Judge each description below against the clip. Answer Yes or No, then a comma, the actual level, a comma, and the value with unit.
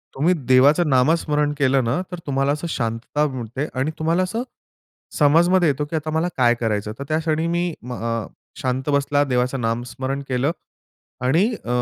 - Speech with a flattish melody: No, average, 4.1 semitones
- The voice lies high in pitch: No, medium, 140 Hz